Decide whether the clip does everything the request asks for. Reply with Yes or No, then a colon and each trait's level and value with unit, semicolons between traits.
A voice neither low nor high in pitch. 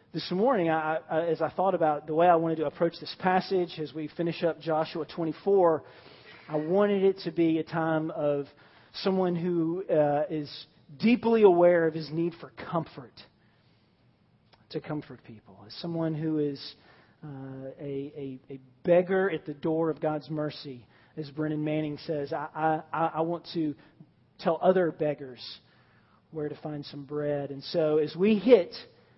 Yes: medium, 155 Hz